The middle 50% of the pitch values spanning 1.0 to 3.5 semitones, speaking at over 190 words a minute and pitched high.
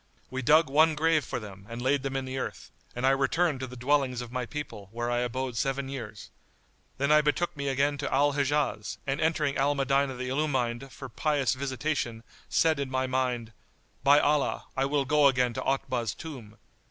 No: narrow, 2.6 semitones; average, 200 wpm; low, 135 Hz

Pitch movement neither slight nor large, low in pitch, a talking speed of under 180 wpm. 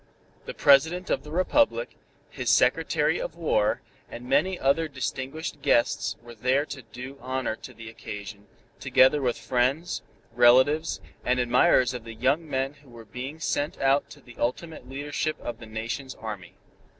Yes: average, 3.7 semitones; low, 130 Hz; average, 160 wpm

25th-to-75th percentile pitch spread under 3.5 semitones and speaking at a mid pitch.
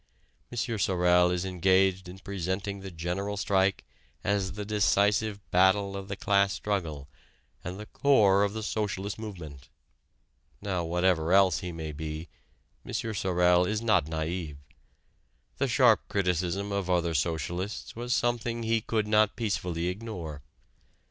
No: average, 2.7 semitones; very low, 95 Hz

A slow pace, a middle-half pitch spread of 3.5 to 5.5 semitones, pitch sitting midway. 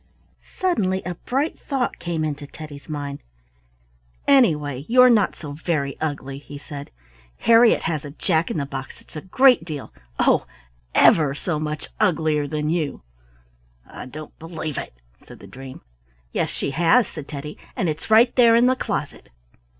No: average, 160 wpm; average, 5.1 semitones; medium, 155 Hz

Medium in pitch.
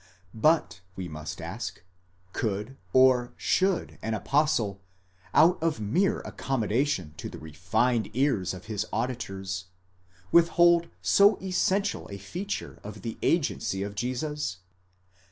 No: low, 115 Hz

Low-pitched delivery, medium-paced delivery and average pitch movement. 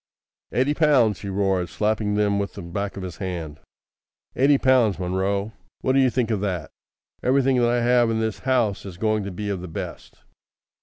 Yes: low, 105 Hz; average, 190 wpm; average, 4.1 semitones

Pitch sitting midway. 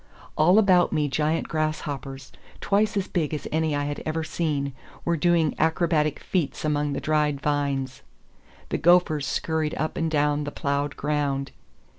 Yes: medium, 150 Hz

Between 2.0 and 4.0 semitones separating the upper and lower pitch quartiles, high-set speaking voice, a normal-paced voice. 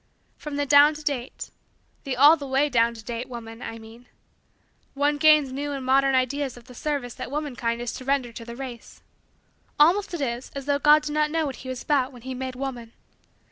No: average, 3.1 semitones; very high, 265 Hz; fast, 220 wpm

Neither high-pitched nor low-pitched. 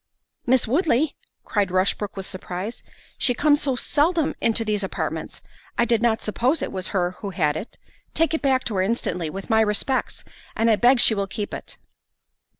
No: high, 225 Hz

